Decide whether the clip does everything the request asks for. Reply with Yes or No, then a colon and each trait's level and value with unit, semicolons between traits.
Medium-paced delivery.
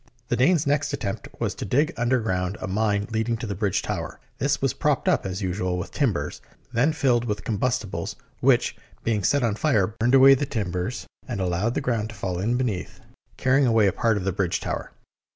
No: fast, 210 wpm